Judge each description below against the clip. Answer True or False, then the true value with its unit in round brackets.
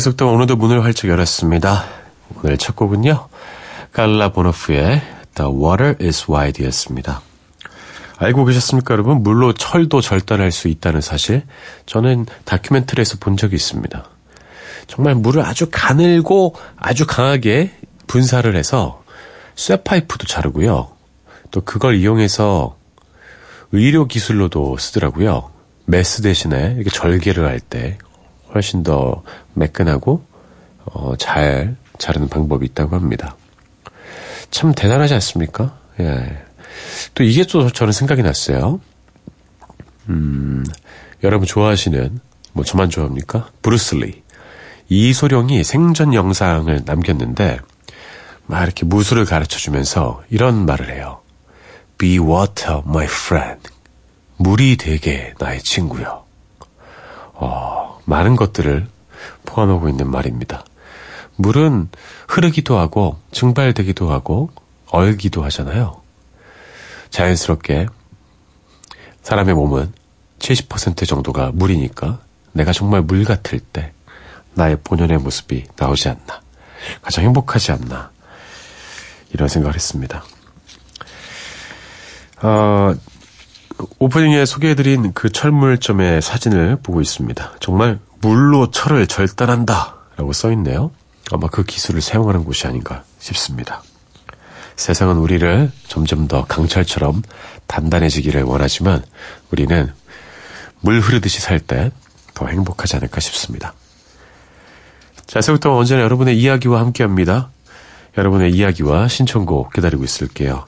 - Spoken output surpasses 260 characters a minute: True (270 characters per minute)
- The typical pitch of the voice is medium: False (95 Hz)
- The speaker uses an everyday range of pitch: False (7.1 semitones)